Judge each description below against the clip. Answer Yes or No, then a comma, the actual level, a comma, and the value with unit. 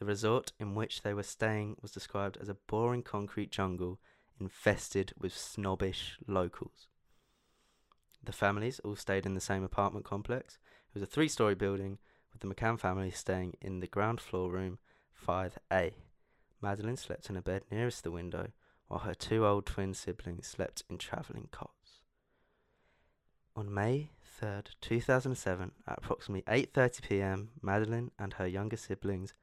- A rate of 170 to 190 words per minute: No, average, 150 wpm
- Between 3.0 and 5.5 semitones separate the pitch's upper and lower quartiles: No, narrow, 2.5 semitones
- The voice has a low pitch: Yes, low, 100 Hz